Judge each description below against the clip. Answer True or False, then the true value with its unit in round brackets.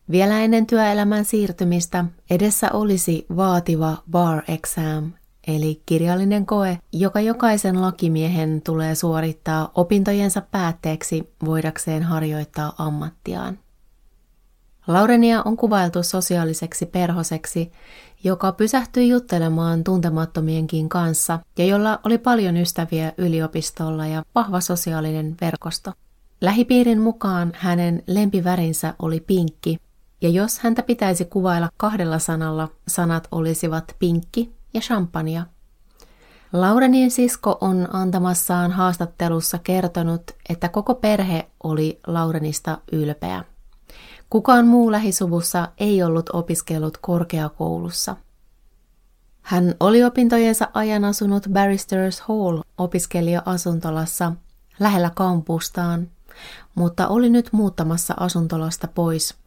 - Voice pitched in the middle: True (175 Hz)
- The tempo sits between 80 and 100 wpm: True (95 wpm)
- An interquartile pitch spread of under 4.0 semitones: True (3.5 semitones)